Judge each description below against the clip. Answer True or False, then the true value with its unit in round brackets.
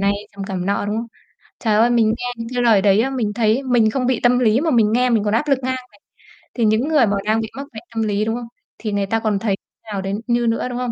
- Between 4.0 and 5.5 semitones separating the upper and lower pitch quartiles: False (2.8 semitones)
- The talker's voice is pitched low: False (225 Hz)